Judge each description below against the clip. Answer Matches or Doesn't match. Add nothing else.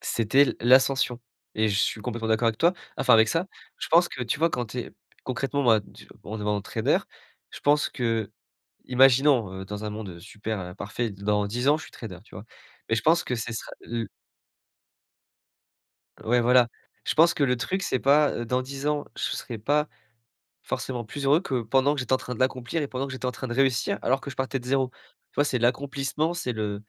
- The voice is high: Doesn't match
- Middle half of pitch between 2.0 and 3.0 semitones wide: Doesn't match